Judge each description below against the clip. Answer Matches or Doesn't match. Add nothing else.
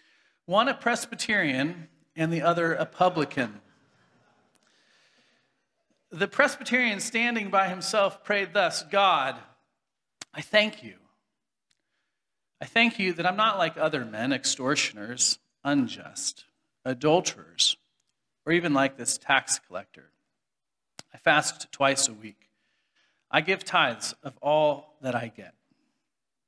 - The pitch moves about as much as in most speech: Doesn't match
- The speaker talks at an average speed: Doesn't match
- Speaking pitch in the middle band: Matches